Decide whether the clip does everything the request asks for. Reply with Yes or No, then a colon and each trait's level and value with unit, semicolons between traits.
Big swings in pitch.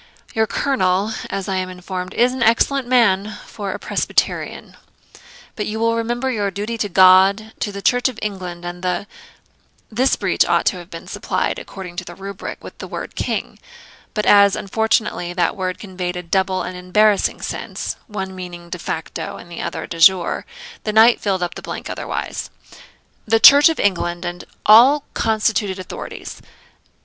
No: average, 3.4 semitones